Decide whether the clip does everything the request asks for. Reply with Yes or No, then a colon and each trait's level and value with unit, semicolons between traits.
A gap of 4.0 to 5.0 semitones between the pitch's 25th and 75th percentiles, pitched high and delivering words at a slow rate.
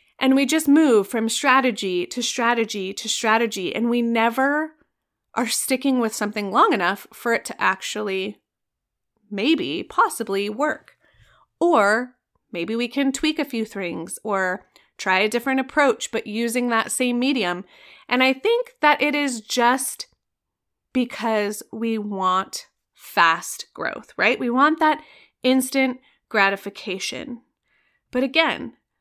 Yes: average, 4.5 semitones; high, 240 Hz; slow, 130 wpm